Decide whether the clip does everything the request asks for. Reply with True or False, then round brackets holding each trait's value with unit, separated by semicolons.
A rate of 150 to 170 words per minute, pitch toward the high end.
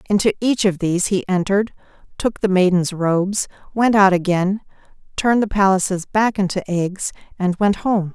True (160 wpm; 195 Hz)